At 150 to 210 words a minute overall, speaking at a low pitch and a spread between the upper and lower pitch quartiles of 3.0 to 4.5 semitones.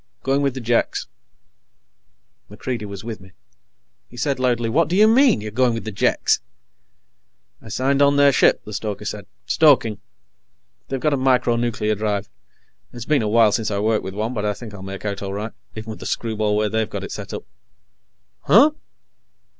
Yes: average, 195 wpm; low, 115 Hz; average, 3.7 semitones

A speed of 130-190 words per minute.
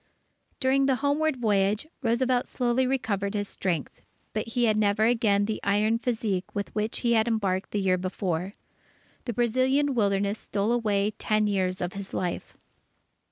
Yes: average, 160 wpm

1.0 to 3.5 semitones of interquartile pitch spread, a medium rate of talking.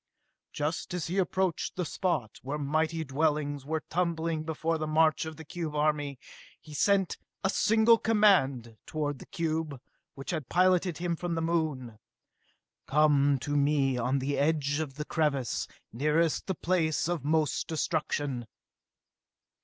Yes: average, 2.8 semitones; average, 145 wpm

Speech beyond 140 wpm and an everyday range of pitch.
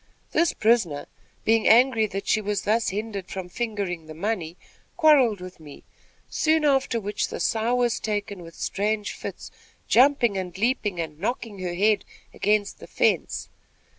Yes: average, 150 wpm; average, 3.9 semitones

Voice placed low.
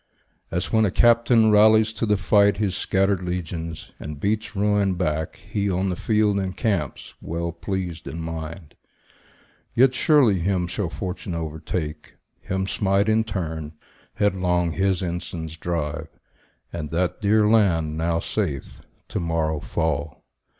Yes: very low, 90 Hz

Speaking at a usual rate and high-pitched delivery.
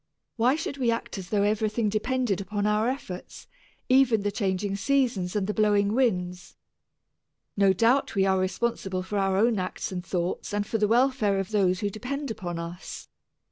Yes: average, 180 wpm; high, 205 Hz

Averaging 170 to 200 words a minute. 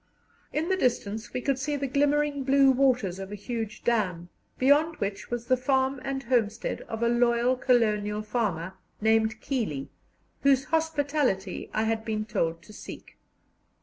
No: average, 155 wpm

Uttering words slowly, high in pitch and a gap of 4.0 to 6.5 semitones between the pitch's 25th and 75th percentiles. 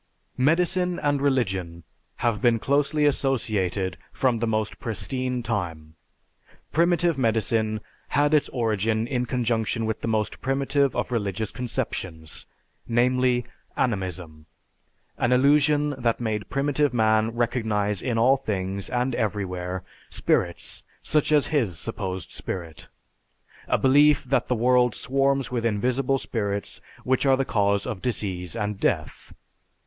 No: slow, 125 wpm; low, 115 Hz; average, 4.7 semitones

